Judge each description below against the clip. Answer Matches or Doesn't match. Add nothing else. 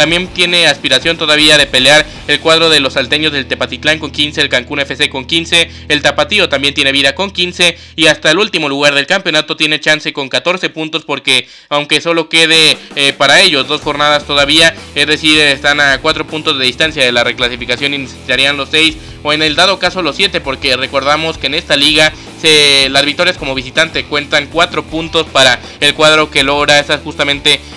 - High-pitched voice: Doesn't match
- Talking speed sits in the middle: Doesn't match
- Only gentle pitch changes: Matches